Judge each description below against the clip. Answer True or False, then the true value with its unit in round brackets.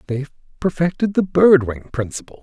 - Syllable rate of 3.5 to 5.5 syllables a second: False (5.7 syllables/s)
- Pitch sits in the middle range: True (145 Hz)